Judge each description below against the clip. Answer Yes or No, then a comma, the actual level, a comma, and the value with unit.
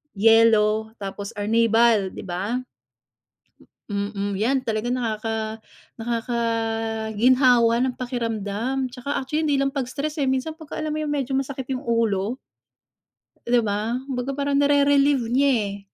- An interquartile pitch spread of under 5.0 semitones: Yes, average, 3.5 semitones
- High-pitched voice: Yes, high, 235 Hz